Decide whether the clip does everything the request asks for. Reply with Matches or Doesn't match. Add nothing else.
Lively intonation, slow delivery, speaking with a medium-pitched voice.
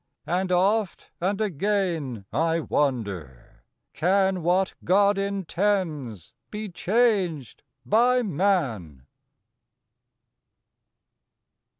Matches